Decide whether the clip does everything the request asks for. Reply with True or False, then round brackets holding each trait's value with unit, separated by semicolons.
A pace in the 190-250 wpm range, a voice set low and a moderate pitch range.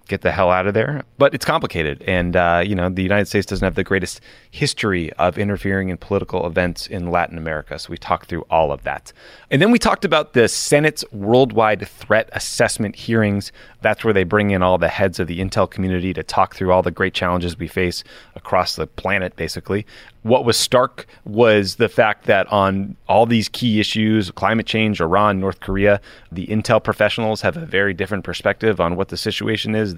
True (205 wpm; 100 Hz; 3.2 semitones)